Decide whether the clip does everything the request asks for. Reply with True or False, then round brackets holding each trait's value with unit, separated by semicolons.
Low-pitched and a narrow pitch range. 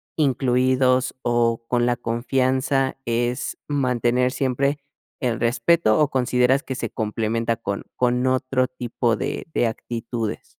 True (125 Hz; 1.8 semitones)